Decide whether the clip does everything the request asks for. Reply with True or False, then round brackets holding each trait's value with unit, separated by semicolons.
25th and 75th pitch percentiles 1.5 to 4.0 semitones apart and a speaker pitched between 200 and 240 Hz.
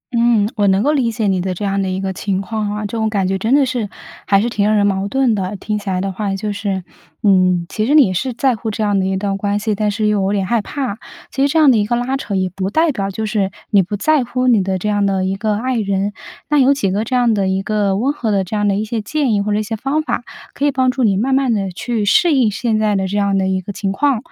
True (3.5 semitones; 210 Hz)